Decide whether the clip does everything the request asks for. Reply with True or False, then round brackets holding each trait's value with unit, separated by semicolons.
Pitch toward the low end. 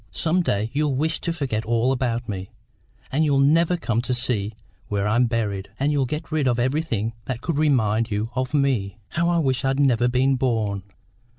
True (125 Hz)